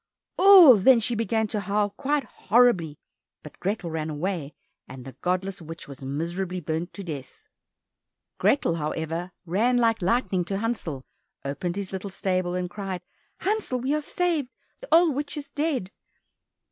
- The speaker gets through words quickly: No, average, 155 wpm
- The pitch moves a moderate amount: No, wide, 6.5 semitones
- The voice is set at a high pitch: Yes, high, 195 Hz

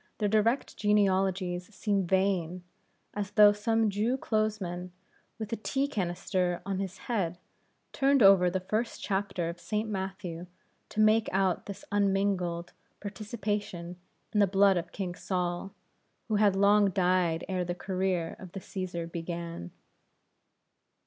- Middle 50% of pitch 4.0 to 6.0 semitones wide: No, narrow, 2.6 semitones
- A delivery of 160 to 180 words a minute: No, slow, 135 wpm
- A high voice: Yes, high, 195 Hz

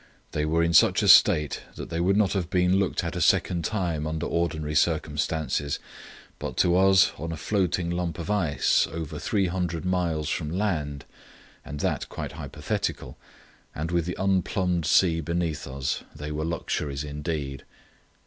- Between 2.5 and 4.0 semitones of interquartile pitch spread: Yes, average, 3.0 semitones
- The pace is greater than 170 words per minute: No, average, 165 wpm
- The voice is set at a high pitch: No, very low, 85 Hz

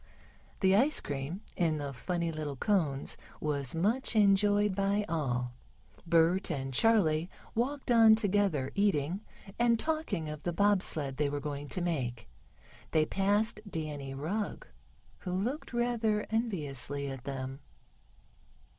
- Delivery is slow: Yes, slow, 130 wpm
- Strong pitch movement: Yes, wide, 6.4 semitones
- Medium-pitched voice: Yes, medium, 175 Hz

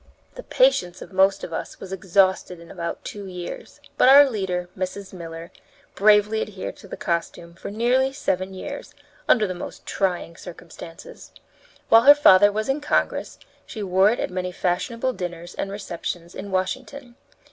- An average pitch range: Yes, average, 3.5 semitones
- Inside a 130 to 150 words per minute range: No, average, 165 wpm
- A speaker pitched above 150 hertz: Yes, high, 190 Hz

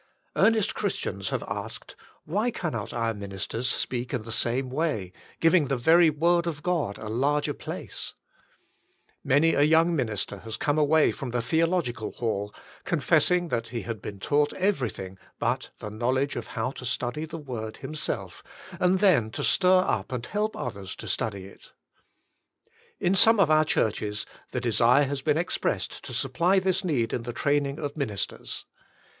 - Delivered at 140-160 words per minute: No, average, 175 wpm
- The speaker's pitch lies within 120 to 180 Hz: Yes, low, 135 Hz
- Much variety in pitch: Yes, wide, 6.2 semitones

